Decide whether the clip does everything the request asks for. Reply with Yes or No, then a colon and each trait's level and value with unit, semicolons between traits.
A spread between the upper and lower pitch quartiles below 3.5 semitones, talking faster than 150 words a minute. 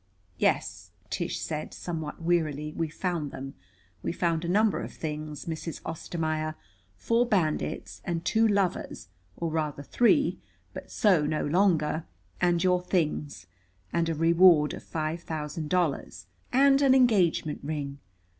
No: average, 3.0 semitones; slow, 135 wpm